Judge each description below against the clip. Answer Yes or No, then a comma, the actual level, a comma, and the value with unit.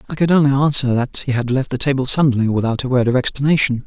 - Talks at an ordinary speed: No, fast, 250 wpm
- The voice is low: Yes, low, 130 Hz